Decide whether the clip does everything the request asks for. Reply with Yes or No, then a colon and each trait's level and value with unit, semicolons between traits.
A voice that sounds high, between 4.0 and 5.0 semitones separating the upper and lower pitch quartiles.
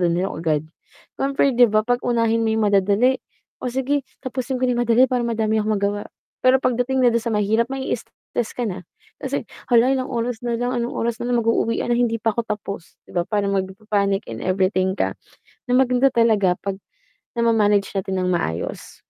No: high, 230 Hz; average, 3.6 semitones